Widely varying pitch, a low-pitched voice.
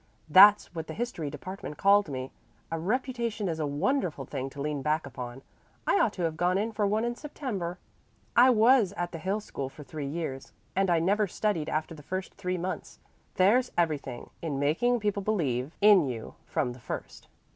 No: wide, 5.9 semitones; medium, 175 Hz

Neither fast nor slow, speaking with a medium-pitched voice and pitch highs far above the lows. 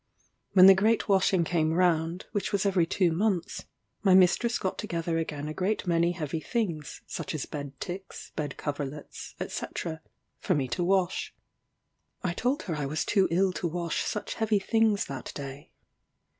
No: average, 170 wpm; medium, 175 Hz; average, 3.8 semitones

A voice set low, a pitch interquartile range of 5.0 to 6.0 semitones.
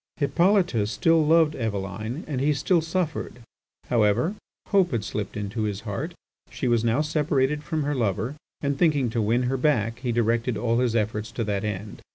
Yes: low, 125 Hz; wide, 5.5 semitones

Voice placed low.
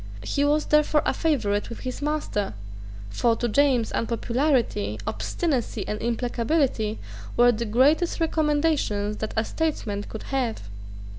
No: high, 245 Hz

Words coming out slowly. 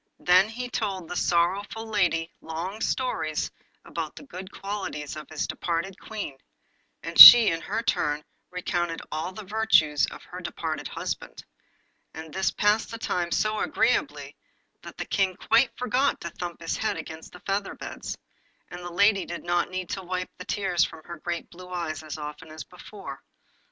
No: average, 170 wpm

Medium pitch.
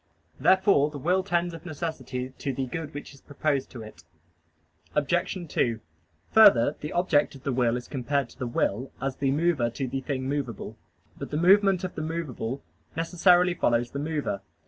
Yes: medium, 145 Hz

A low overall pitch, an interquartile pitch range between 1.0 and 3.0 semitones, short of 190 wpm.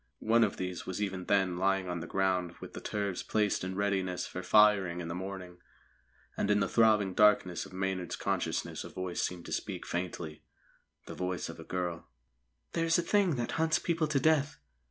No: very low, 95 Hz; average, 2.7 semitones; average, 195 wpm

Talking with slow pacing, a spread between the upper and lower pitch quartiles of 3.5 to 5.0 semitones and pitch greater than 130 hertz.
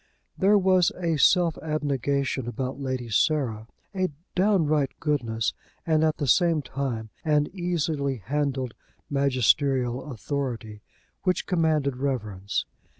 Yes: slow, 110 wpm; average, 4.0 semitones; medium, 140 Hz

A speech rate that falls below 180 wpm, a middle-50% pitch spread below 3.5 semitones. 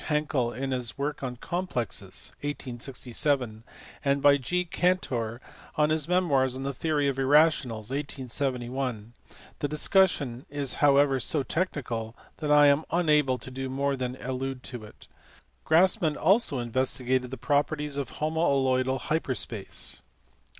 Yes: slow, 135 wpm; average, 3.0 semitones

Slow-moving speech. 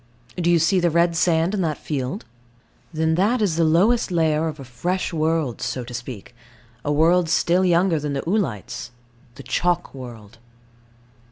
No: average, 170 wpm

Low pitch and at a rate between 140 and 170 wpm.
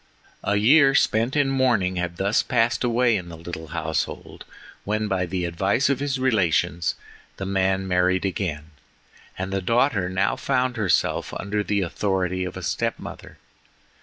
Yes: very low, 95 Hz; average, 160 wpm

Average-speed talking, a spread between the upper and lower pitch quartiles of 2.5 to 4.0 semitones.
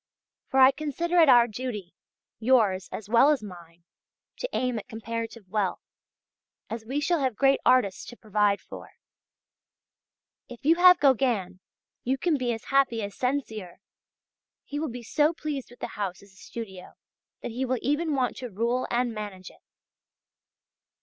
No: average, 165 wpm; average, 4.6 semitones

